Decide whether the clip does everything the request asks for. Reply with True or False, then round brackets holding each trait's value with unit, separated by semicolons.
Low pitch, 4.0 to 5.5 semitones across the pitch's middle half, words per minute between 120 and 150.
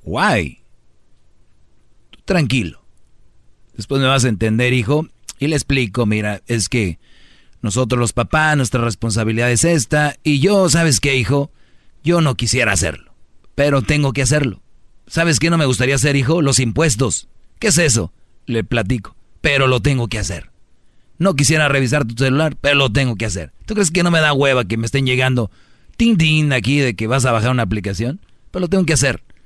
False (130 Hz; 4.5 semitones; 185 wpm)